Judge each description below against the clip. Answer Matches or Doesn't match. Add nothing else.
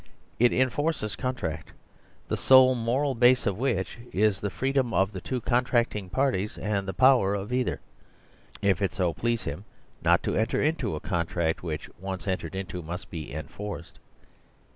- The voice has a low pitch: Matches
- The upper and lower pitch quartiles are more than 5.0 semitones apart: Matches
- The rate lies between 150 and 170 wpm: Matches